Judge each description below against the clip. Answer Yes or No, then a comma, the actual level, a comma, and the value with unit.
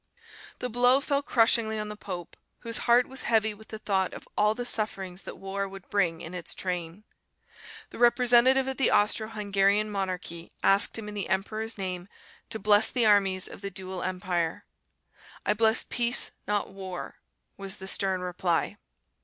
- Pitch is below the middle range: No, high, 205 Hz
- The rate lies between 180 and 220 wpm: No, average, 170 wpm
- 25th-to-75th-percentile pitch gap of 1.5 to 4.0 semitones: Yes, average, 2.9 semitones